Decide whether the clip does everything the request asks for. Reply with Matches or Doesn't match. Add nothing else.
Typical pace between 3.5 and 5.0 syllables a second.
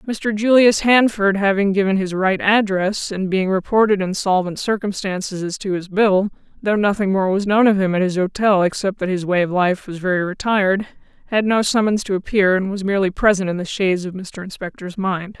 Doesn't match